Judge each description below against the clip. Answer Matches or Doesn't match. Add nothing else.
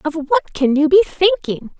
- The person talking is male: Doesn't match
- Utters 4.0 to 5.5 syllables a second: Matches